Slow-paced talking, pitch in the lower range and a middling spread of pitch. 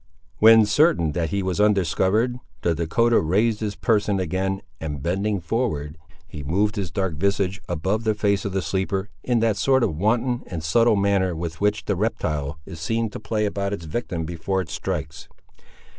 No: average, 180 wpm; low, 100 Hz; average, 4.1 semitones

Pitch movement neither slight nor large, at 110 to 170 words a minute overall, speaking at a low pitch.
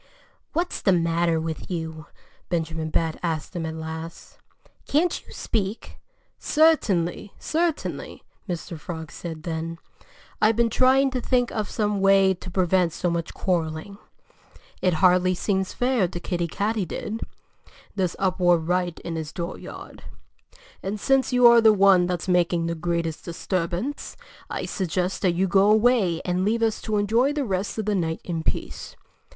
No: average, 4.1 semitones; average, 155 wpm; medium, 185 Hz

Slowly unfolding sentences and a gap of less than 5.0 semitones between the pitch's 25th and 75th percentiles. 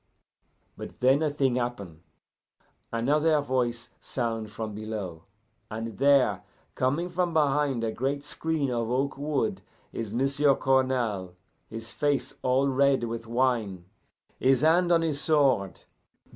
Yes: slow, 130 wpm; average, 3.9 semitones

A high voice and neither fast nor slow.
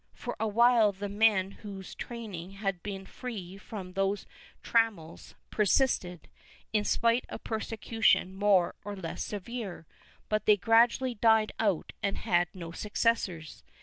No: high, 205 Hz; slow, 130 wpm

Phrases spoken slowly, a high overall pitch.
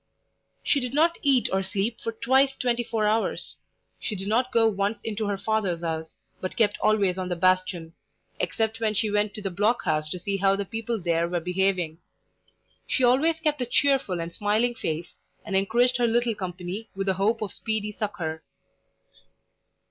No: average, 185 wpm; high, 210 Hz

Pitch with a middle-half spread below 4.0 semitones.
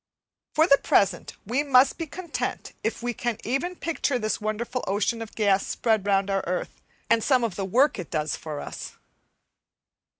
No: average, 4.9 semitones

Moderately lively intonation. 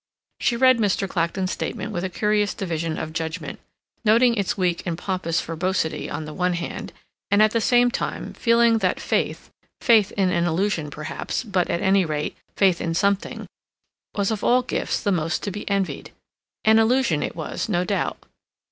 Yes: average, 4.1 semitones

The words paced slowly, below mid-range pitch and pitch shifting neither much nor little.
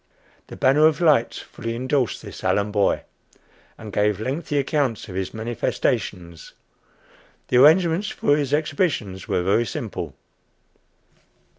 No: slow, 125 wpm; low, 125 Hz; wide, 6.3 semitones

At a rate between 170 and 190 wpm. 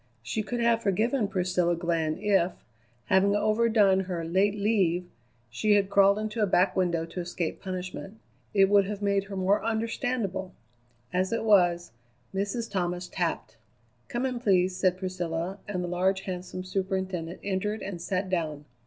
No: average, 155 wpm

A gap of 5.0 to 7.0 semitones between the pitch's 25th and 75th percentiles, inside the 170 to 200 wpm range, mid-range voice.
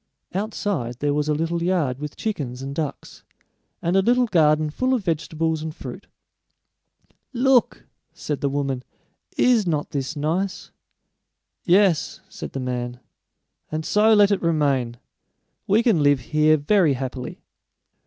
No: wide, 5.4 semitones; average, 140 wpm; medium, 155 Hz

